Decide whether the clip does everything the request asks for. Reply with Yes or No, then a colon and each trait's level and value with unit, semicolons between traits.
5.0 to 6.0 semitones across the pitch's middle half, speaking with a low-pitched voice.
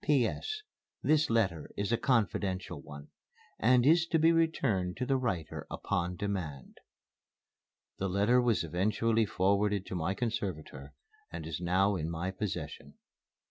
Yes: wide, 5.5 semitones; low, 100 Hz